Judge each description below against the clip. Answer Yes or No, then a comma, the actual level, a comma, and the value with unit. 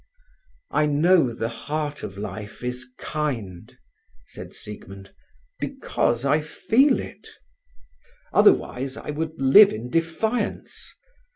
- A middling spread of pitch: No, wide, 5.9 semitones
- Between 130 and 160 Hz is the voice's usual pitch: Yes, medium, 140 Hz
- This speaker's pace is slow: Yes, slow, 105 wpm